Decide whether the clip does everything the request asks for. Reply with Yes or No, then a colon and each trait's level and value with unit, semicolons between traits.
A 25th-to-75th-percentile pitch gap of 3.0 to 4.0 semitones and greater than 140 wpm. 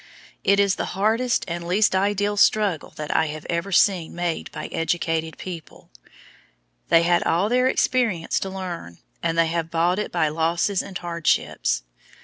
Yes: average, 3.3 semitones; average, 160 wpm